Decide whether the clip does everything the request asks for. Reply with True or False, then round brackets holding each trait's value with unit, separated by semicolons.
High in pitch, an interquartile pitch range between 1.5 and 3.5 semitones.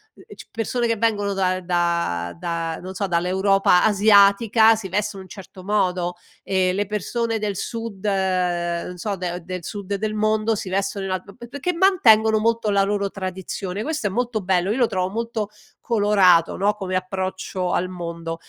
True (195 Hz; 2.8 semitones)